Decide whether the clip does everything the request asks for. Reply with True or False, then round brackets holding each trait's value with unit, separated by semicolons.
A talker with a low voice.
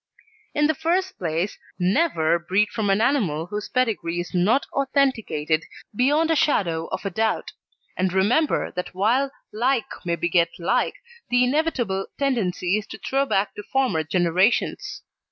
False (210 Hz)